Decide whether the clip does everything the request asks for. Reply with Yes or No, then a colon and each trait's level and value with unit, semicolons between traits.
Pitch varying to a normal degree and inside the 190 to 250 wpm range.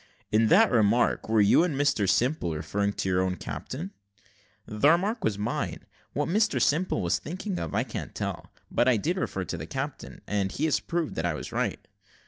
No: wide, 8.3 semitones; average, 200 wpm